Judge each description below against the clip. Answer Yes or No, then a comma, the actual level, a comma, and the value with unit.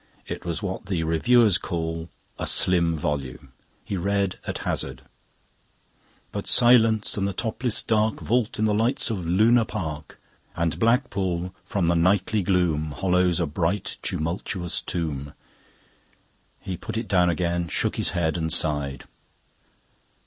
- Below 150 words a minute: Yes, average, 140 wpm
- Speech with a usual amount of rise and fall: Yes, average, 4.1 semitones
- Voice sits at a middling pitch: No, very low, 90 Hz